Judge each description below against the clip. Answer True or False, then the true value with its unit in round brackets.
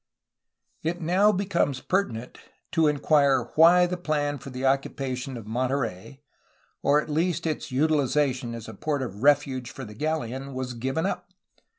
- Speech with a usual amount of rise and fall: True (3.8 semitones)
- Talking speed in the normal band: True (165 wpm)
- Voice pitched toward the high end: False (140 Hz)